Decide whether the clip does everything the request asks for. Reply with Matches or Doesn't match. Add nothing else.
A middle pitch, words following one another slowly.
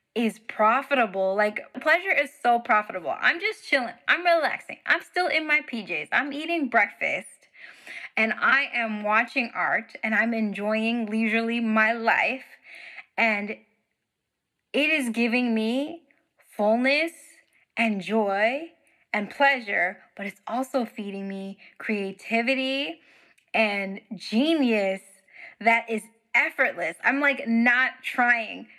Doesn't match